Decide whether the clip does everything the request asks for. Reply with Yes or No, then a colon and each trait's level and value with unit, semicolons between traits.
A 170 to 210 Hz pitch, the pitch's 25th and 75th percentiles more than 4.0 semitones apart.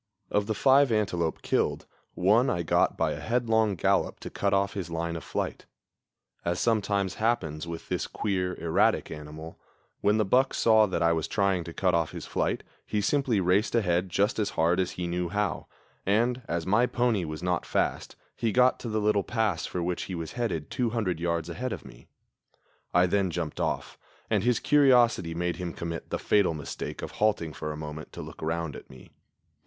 No: very low, 95 Hz; average, 4.6 semitones